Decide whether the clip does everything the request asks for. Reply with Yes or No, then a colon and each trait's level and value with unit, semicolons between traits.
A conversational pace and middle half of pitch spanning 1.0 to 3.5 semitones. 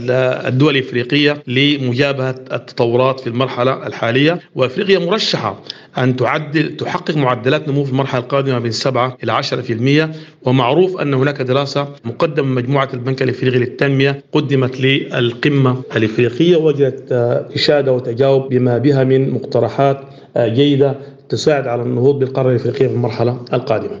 Yes: average, 125 wpm; narrow, 2.4 semitones